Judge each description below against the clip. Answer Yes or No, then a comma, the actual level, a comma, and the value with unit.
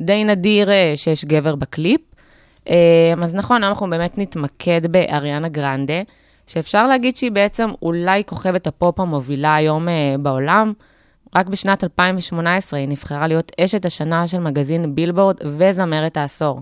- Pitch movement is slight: No, average, 4.1 semitones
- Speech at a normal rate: Yes, average, 125 wpm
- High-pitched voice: No, medium, 170 Hz